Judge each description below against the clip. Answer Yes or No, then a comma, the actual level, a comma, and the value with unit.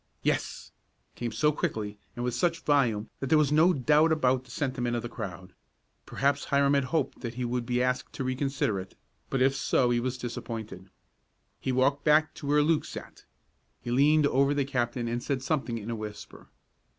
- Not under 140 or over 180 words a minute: No, average, 195 wpm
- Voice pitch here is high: No, low, 130 Hz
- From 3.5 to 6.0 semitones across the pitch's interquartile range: No, average, 3.1 semitones